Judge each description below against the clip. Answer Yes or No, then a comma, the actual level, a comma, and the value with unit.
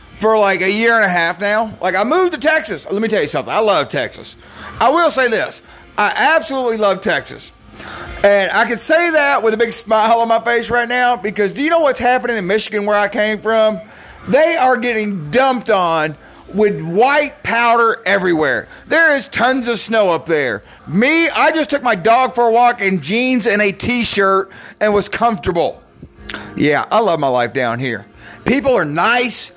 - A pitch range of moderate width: Yes, average, 3.6 semitones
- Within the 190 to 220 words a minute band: Yes, average, 200 wpm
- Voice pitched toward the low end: No, high, 230 Hz